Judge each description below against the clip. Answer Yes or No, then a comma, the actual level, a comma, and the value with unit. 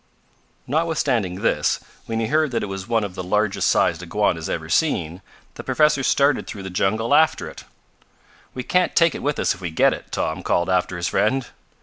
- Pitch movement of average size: No, wide, 7.3 semitones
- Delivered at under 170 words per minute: No, average, 200 wpm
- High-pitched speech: No, low, 110 Hz